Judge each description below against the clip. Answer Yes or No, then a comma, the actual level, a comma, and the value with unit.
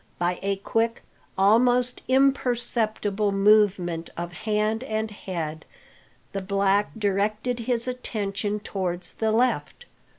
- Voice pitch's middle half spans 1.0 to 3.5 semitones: Yes, average, 2.8 semitones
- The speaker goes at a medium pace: No, slow, 105 wpm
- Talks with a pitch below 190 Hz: No, high, 210 Hz